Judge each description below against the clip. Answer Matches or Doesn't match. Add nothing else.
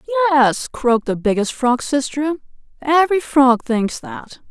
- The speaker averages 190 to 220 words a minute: Doesn't match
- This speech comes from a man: Doesn't match